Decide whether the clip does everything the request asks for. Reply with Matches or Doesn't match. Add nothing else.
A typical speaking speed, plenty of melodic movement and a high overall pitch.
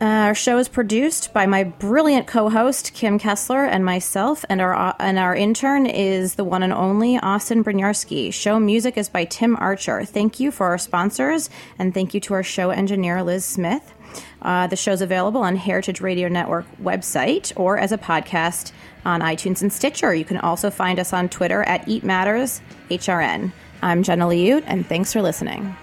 Doesn't match